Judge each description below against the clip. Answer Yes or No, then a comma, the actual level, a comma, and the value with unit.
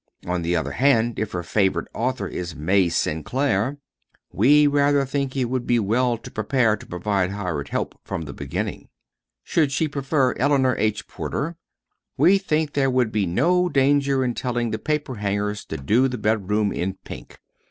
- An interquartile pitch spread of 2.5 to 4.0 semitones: No, wide, 5.6 semitones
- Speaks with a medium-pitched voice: No, low, 120 Hz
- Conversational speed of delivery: Yes, average, 175 wpm